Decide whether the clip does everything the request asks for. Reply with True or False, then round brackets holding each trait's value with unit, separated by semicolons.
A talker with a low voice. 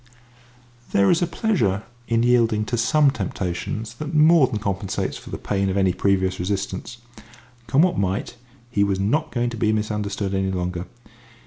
True (105 Hz)